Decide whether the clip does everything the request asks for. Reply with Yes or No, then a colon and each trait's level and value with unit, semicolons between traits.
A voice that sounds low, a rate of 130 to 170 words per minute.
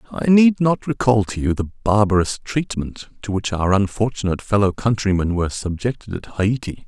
Yes: low, 105 Hz; average, 165 wpm